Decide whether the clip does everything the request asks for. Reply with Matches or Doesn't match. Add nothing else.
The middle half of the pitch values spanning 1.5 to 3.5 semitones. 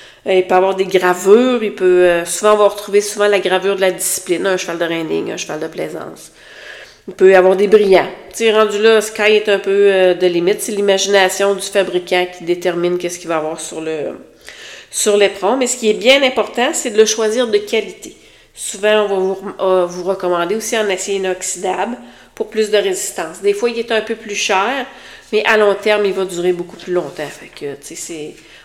Matches